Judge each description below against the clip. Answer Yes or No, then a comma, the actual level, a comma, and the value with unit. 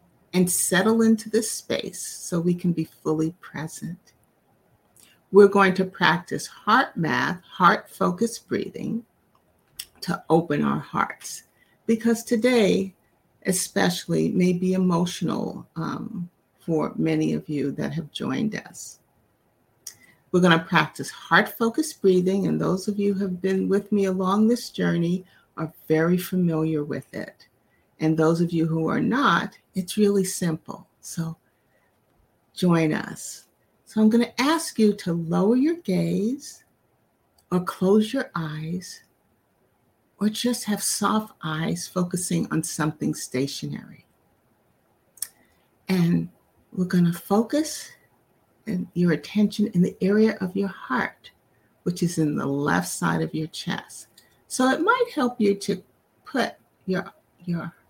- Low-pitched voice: No, medium, 185 Hz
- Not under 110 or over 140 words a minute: Yes, slow, 135 wpm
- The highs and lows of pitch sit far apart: No, average, 4.1 semitones